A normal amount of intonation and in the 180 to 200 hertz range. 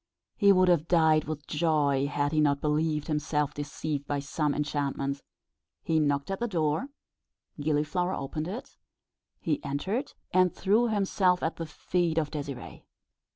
No: average, 3.6 semitones; medium, 155 Hz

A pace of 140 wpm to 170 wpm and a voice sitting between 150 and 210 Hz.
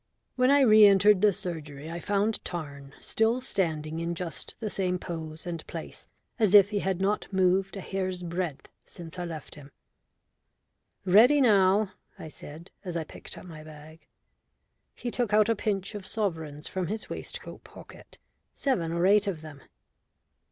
Yes: average, 165 wpm; medium, 185 Hz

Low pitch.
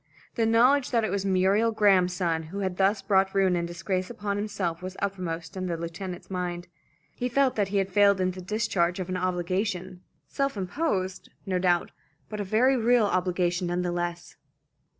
No: high, 190 Hz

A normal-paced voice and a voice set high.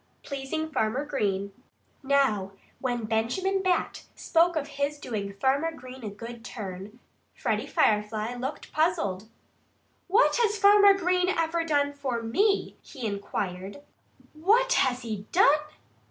No: slow, 130 wpm; very high, 270 Hz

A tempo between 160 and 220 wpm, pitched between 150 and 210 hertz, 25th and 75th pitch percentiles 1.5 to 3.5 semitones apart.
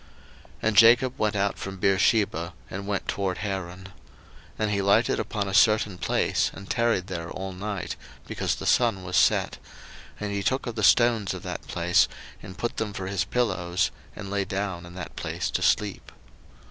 No: average, 185 wpm; low, 100 Hz; narrow, 2.4 semitones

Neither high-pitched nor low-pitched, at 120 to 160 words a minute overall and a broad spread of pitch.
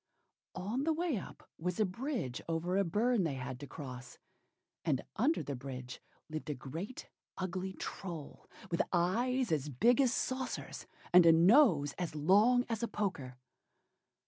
Yes: medium, 180 Hz; average, 155 wpm; wide, 8.1 semitones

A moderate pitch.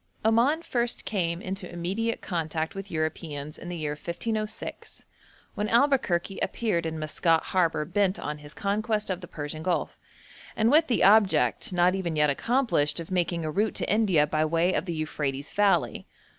Yes: medium, 175 Hz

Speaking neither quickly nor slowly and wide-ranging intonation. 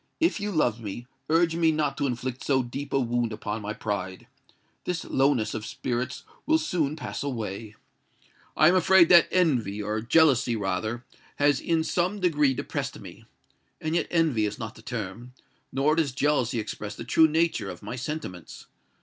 Yes: average, 165 wpm; wide, 6.3 semitones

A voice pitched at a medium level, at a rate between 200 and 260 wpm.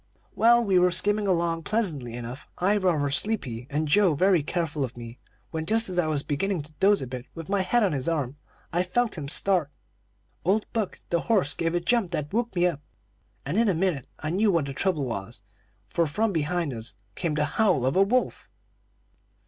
Yes: medium, 170 Hz; fast, 205 wpm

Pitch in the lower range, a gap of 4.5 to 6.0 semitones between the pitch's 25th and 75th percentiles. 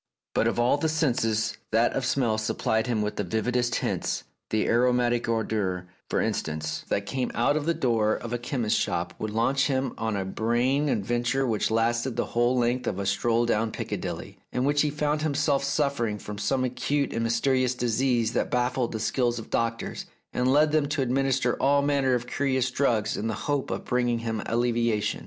No: low, 120 Hz; average, 3.1 semitones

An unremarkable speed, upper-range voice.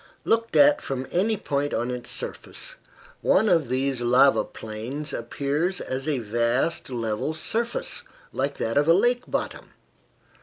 No: average, 145 wpm; medium, 140 Hz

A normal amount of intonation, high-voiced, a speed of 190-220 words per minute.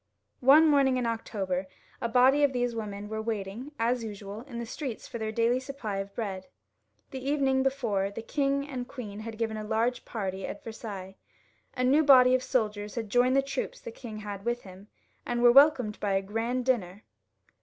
Yes: average, 3.8 semitones; high, 230 Hz; average, 195 wpm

